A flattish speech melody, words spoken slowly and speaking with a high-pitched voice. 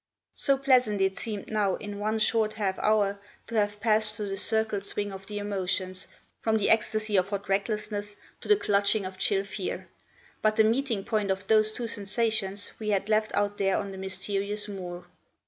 No: narrow, 1.7 semitones; average, 190 wpm; high, 205 Hz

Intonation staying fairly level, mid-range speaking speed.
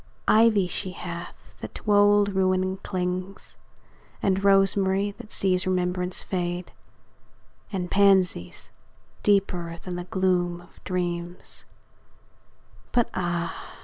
No: narrow, 1.7 semitones; slow, 105 wpm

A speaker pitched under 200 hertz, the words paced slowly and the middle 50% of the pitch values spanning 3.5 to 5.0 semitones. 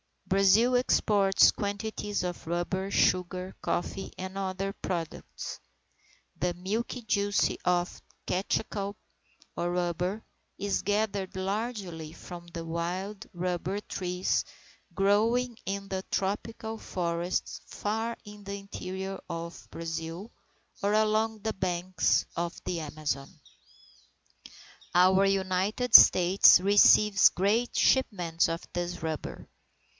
No: high, 190 Hz; slow, 105 wpm; average, 2.7 semitones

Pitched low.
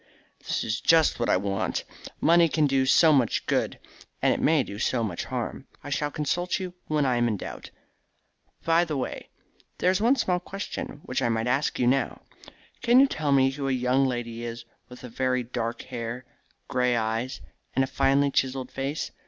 Yes: low, 130 Hz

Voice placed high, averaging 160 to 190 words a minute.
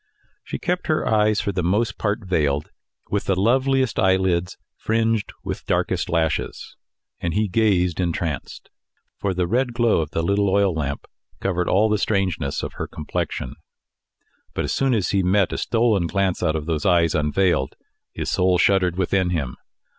No: very low, 95 Hz; average, 170 wpm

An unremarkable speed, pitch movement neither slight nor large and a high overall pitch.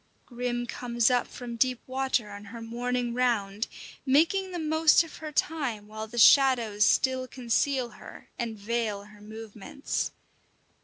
Yes: average, 145 wpm; average, 3.3 semitones; high, 240 Hz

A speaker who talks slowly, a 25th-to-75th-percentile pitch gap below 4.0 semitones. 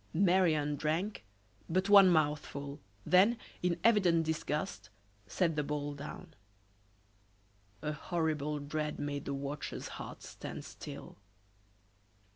Yes: slow, 110 wpm; average, 3.6 semitones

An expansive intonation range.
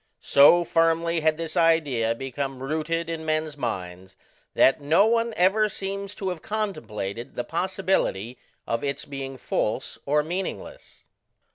No: average, 5.0 semitones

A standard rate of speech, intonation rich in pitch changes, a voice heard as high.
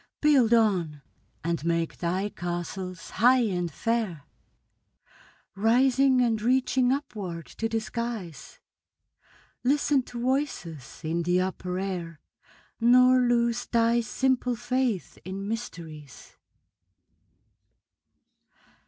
No: slow, 95 wpm; wide, 5.9 semitones; high, 225 Hz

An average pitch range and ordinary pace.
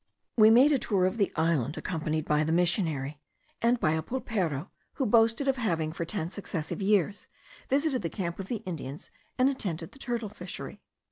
No: wide, 6.3 semitones; average, 185 wpm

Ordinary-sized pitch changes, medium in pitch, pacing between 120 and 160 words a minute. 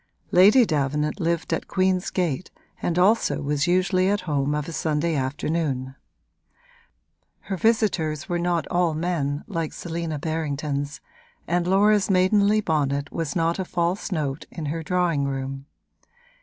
Yes: average, 3.7 semitones; medium, 165 Hz; average, 140 wpm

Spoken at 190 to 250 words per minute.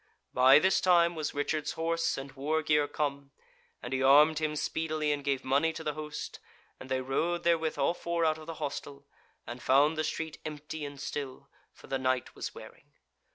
Yes: average, 195 wpm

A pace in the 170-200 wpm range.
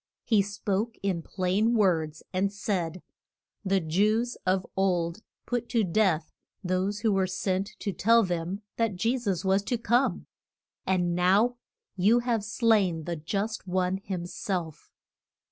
No: average, 145 wpm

